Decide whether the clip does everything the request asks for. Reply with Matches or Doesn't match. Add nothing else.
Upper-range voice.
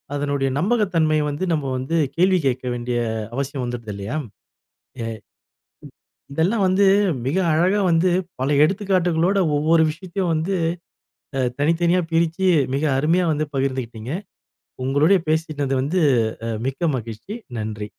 Doesn't match